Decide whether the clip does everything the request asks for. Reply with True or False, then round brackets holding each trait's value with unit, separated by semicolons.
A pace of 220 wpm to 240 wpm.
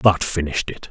False (200 wpm)